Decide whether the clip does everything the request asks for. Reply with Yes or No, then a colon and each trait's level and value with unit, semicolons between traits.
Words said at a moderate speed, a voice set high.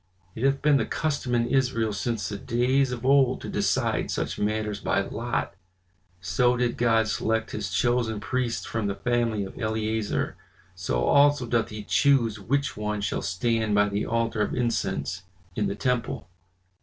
No: average, 170 wpm; low, 115 Hz